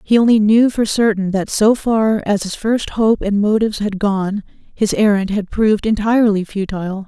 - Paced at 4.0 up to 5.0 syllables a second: Yes, 4.9 syllables/s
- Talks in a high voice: Yes, high, 210 Hz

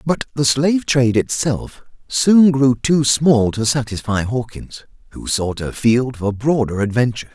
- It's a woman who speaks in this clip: No, male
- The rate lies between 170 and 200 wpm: No, average, 155 wpm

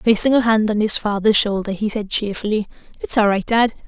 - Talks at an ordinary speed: No, fast, 215 wpm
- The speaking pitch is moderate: No, high, 215 Hz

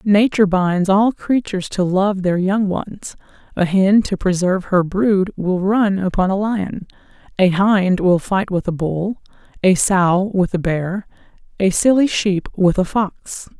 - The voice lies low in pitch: No, high, 190 Hz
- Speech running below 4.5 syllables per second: Yes, 4.0 syllables/s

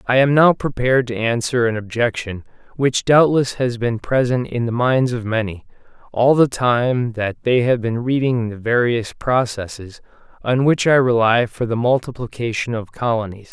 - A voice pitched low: Yes, low, 120 Hz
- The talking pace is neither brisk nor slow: Yes, average, 170 wpm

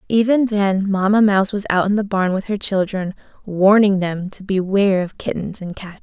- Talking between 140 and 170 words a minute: No, average, 200 wpm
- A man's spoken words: No, female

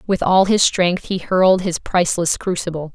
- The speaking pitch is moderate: Yes, medium, 180 Hz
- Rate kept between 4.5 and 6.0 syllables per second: Yes, 5.0 syllables/s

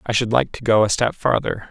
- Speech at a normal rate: No, fast, 280 wpm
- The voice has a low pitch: Yes, low, 115 Hz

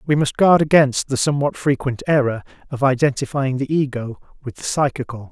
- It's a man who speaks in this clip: Yes, male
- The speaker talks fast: No, average, 170 wpm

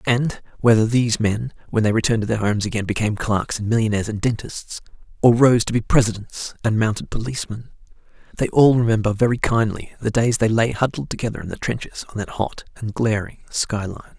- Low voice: Yes, low, 110 Hz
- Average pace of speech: Yes, average, 195 wpm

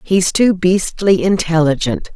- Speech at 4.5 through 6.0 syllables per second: No, 3.9 syllables/s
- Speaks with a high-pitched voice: No, medium, 175 Hz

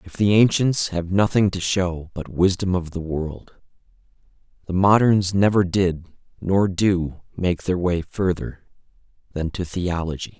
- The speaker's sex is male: Yes, male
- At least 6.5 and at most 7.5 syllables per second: No, 4.0 syllables/s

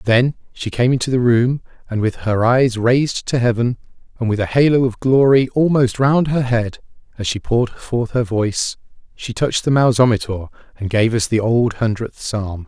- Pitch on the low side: Yes, low, 120 Hz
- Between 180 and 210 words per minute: Yes, average, 190 wpm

